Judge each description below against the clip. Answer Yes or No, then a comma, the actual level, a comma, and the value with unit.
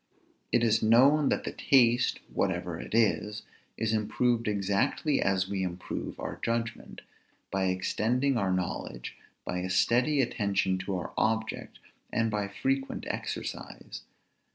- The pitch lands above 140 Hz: No, low, 110 Hz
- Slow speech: Yes, slow, 130 wpm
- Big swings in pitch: No, average, 3.8 semitones